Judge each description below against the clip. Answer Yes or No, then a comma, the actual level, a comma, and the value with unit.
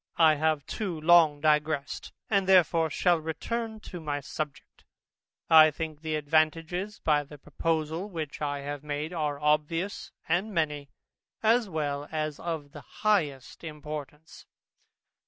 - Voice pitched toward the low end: No, medium, 155 Hz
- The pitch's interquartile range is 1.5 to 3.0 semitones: Yes, narrow, 2.4 semitones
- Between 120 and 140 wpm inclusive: Yes, slow, 135 wpm